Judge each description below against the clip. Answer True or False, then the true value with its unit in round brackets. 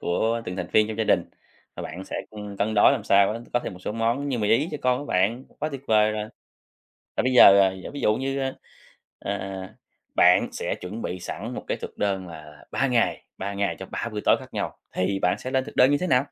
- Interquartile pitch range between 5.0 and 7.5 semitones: False (4.6 semitones)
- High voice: False (110 Hz)